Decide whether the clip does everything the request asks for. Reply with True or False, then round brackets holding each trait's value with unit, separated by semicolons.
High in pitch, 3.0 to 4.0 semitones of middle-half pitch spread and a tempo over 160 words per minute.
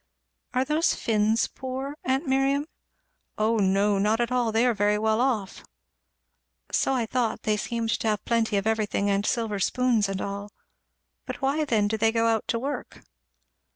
True (225 Hz; 3.3 semitones; 175 wpm)